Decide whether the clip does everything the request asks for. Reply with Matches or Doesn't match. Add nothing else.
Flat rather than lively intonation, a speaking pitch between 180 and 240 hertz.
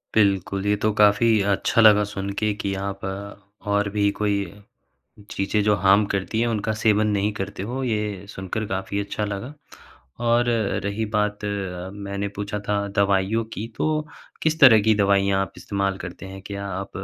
Doesn't match